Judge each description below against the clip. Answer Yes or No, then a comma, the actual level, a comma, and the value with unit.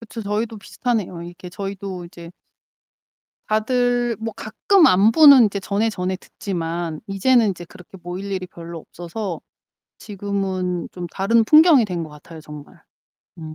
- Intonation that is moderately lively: Yes, average, 4.2 semitones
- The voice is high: Yes, high, 195 Hz